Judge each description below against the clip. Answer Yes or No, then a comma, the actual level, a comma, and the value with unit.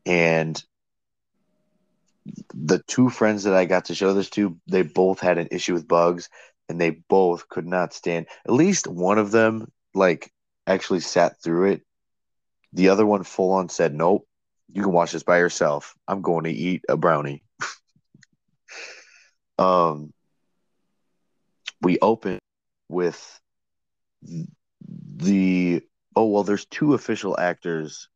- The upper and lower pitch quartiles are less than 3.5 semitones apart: No, average, 4.5 semitones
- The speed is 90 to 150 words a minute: Yes, slow, 135 wpm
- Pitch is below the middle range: Yes, very low, 95 Hz